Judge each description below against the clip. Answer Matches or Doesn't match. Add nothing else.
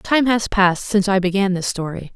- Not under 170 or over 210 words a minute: Doesn't match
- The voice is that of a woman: Matches